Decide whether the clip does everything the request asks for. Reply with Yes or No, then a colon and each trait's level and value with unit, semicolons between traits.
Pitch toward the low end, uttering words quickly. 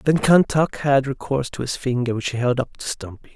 Yes: low, 130 Hz; fast, 235 wpm